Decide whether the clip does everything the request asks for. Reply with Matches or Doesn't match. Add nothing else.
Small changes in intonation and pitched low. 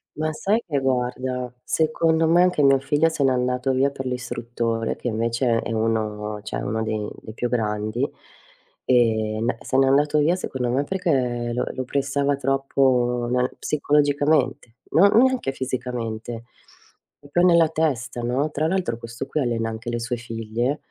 Doesn't match